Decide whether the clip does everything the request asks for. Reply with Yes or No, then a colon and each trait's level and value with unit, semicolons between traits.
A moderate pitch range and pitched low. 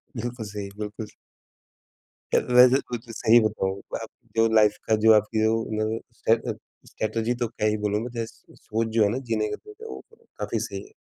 No: narrow, 1.7 semitones; low, 110 Hz